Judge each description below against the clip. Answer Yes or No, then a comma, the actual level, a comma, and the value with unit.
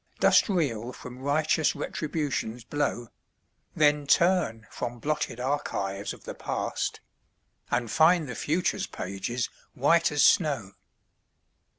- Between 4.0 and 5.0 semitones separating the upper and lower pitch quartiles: Yes, average, 4.6 semitones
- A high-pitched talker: No, medium, 140 Hz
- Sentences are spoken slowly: Yes, slow, 110 wpm